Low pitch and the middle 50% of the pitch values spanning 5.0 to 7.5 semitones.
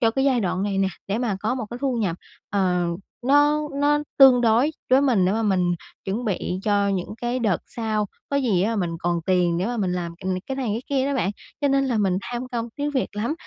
No: high, 225 Hz; wide, 5.4 semitones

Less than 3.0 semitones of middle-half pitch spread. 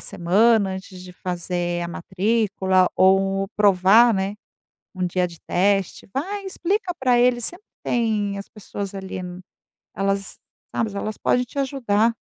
No: average, 3.9 semitones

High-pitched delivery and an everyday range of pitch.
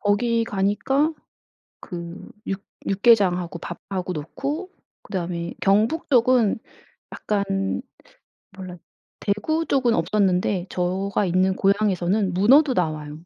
Yes: high, 195 Hz; average, 4.1 semitones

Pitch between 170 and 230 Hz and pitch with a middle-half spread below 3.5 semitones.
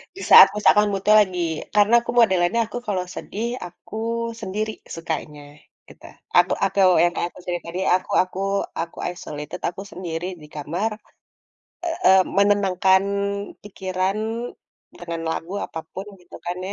Yes: medium, 185 Hz; average, 2.7 semitones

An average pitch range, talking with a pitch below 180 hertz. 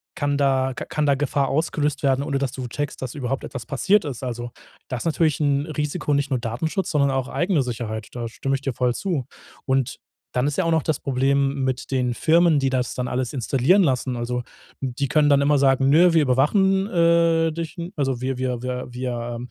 Yes: average, 3.1 semitones; low, 135 Hz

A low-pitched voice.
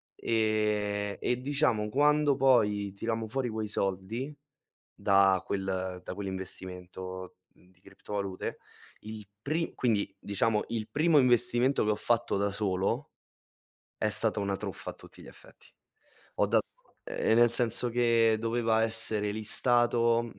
Yes: low, 110 Hz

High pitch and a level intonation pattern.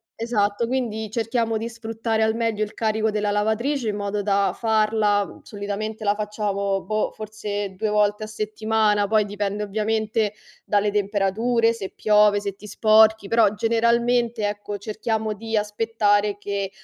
Yes: high, 215 Hz; narrow, 1.4 semitones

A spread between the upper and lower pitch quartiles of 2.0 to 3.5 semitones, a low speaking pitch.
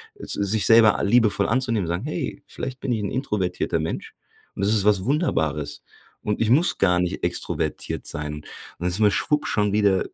No: average, 4.5 semitones; low, 105 Hz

